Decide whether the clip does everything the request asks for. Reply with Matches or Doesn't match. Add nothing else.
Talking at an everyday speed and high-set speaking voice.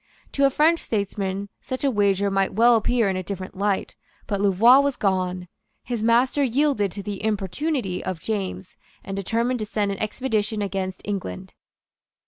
Matches